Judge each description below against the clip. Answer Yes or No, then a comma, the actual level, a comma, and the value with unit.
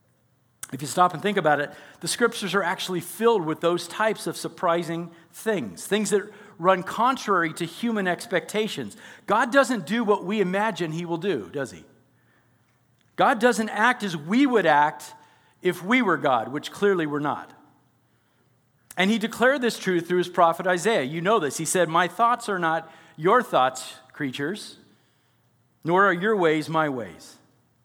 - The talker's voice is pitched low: No, medium, 175 Hz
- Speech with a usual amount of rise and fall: No, wide, 5.9 semitones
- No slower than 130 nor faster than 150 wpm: No, average, 170 wpm